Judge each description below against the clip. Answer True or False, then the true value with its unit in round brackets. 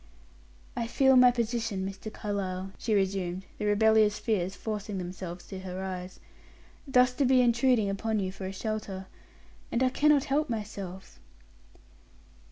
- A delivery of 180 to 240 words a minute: False (145 wpm)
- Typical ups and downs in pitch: True (3.9 semitones)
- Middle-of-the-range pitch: False (210 Hz)